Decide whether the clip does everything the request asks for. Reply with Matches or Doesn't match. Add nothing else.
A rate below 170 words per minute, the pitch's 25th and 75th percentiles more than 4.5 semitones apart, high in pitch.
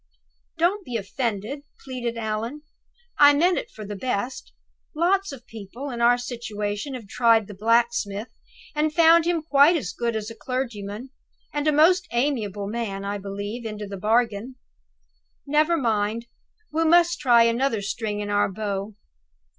Matches